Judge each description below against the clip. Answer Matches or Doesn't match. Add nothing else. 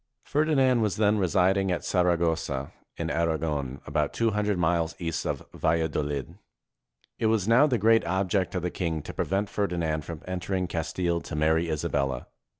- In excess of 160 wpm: Doesn't match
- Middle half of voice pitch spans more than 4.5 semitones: Doesn't match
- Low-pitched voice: Matches